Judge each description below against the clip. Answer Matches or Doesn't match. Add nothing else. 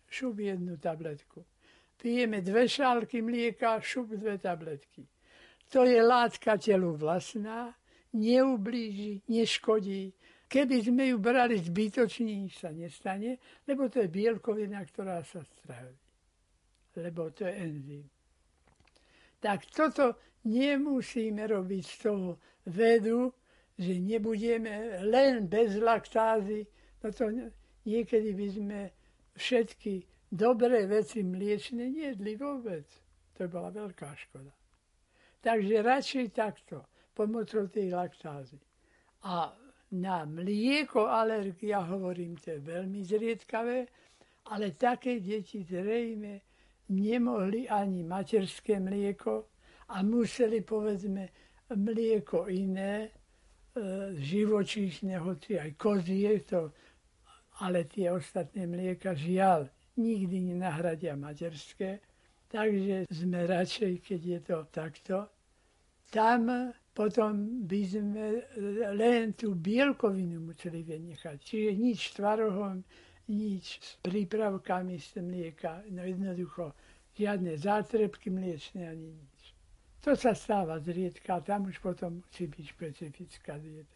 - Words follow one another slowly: Matches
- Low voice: Doesn't match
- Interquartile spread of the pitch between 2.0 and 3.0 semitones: Doesn't match